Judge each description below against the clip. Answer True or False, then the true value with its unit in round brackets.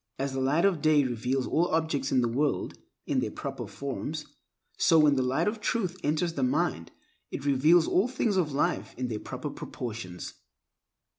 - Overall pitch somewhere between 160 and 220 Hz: False (145 Hz)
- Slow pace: False (190 wpm)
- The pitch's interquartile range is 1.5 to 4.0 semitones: False (4.5 semitones)